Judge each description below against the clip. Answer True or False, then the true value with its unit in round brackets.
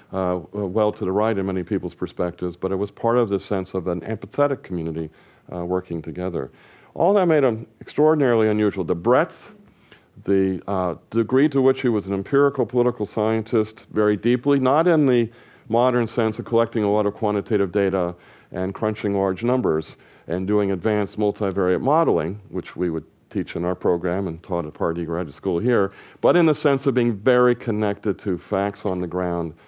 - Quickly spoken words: False (190 wpm)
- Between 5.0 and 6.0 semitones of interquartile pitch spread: False (4.3 semitones)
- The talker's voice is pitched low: True (105 Hz)